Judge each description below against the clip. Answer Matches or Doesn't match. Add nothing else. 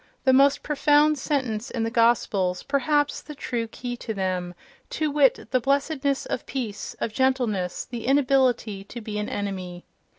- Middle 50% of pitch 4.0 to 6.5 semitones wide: Matches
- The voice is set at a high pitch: Matches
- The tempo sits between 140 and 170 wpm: Matches